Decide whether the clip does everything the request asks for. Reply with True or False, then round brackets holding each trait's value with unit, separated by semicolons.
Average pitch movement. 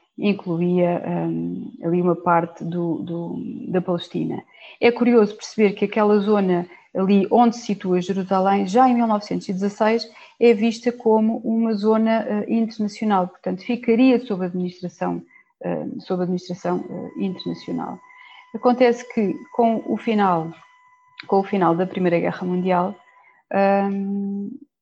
True (4.3 semitones)